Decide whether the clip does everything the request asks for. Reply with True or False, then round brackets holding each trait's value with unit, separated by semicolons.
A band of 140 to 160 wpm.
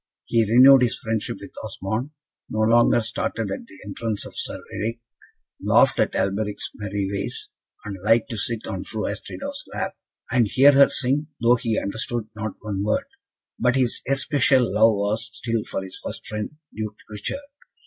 False (170 wpm)